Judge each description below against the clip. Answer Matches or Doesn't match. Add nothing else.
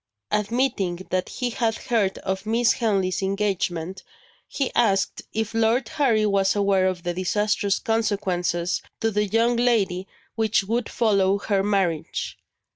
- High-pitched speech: Matches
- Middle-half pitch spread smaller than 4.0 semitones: Matches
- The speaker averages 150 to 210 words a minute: Doesn't match